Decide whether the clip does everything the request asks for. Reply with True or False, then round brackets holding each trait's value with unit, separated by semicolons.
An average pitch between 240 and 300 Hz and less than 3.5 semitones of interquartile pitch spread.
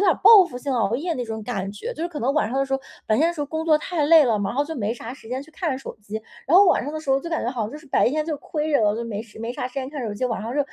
False (270 Hz; 5.2 semitones)